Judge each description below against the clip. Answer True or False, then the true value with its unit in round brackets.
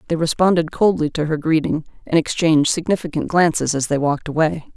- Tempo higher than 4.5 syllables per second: True (6.1 syllables/s)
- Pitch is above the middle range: False (160 Hz)